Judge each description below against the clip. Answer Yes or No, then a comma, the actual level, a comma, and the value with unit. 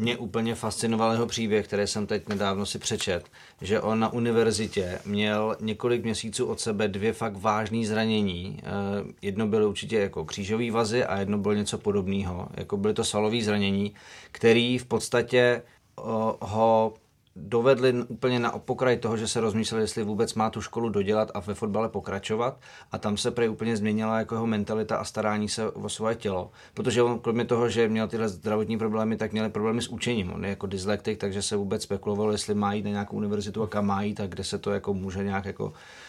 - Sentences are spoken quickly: Yes, fast, 195 wpm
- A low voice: Yes, low, 110 Hz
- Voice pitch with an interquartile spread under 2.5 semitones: Yes, narrow, 1.8 semitones